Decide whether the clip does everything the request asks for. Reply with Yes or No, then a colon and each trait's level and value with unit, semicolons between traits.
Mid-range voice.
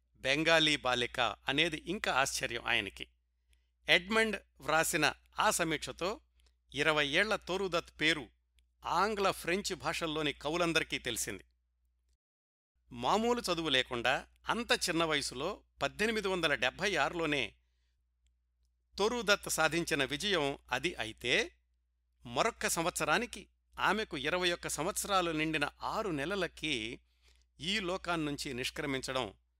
Yes: medium, 150 Hz